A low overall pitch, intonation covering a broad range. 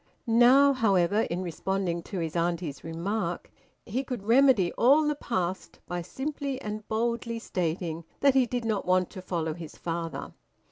No: high, 195 Hz; wide, 5.8 semitones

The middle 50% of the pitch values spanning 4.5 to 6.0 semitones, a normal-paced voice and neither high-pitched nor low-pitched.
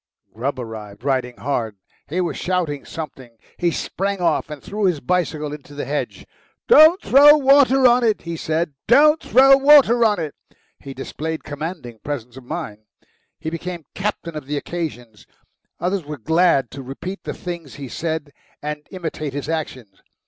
Yes: average, 5.3 semitones; average, 165 wpm; medium, 160 Hz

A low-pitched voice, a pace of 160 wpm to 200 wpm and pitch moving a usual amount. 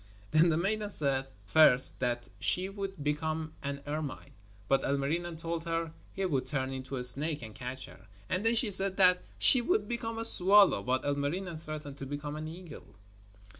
No: medium, 155 Hz; average, 180 wpm; average, 5.0 semitones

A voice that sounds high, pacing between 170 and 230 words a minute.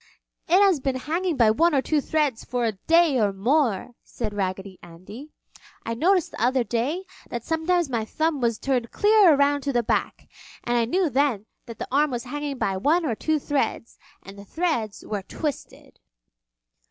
Yes: very high, 265 Hz; average, 185 wpm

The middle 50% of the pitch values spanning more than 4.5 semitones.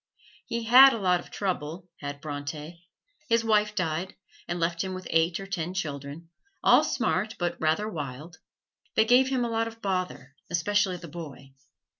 Yes: average, 4.9 semitones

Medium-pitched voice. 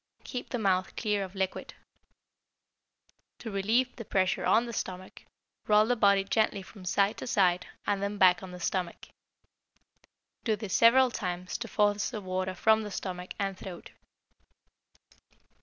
No: high, 200 Hz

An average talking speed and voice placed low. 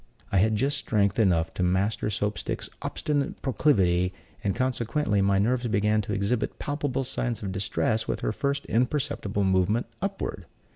Yes: average, 155 wpm; low, 105 Hz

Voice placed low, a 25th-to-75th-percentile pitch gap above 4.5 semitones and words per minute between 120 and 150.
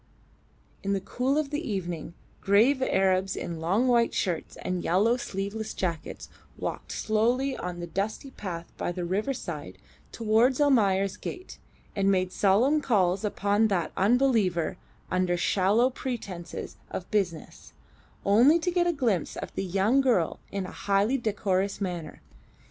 No: high, 200 Hz; average, 4.9 semitones; average, 145 wpm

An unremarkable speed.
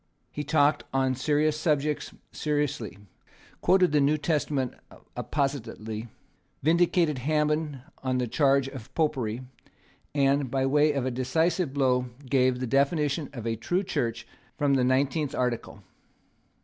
No: slow, 130 wpm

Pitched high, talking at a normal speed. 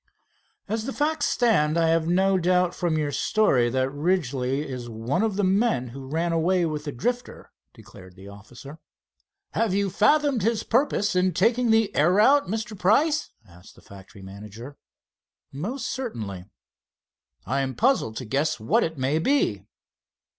No: medium, 165 Hz; average, 160 wpm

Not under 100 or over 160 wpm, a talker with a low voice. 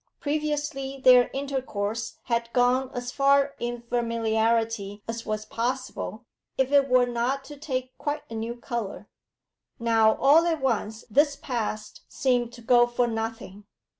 No: average, 140 wpm; high, 245 Hz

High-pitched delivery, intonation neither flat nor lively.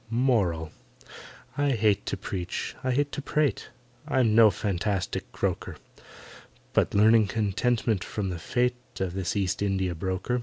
No: low, 105 Hz; average, 4.5 semitones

